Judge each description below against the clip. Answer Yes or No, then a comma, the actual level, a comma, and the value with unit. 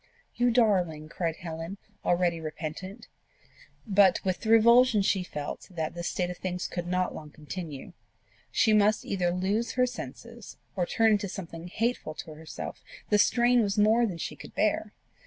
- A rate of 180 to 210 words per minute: No, average, 165 wpm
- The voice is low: No, medium, 185 Hz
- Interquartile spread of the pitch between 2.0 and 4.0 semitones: No, average, 4.5 semitones